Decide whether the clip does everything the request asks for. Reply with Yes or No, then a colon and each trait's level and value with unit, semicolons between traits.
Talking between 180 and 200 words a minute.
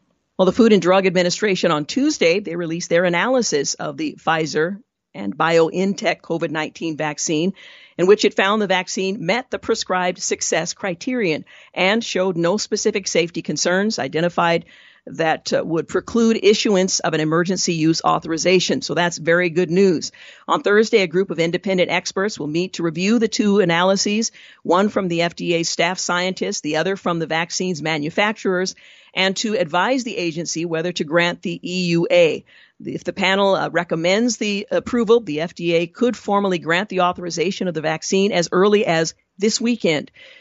No: average, 160 wpm